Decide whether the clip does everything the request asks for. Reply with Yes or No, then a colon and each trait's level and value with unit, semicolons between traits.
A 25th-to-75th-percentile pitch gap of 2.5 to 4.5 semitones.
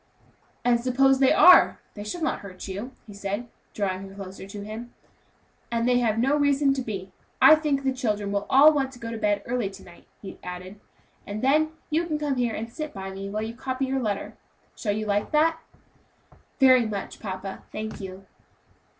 No: average, 5.0 semitones